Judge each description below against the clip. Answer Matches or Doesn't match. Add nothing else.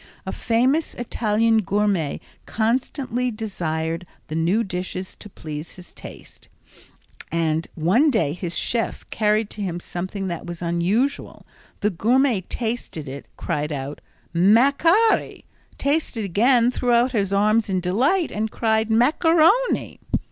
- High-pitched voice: Matches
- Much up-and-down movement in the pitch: Matches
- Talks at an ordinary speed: Doesn't match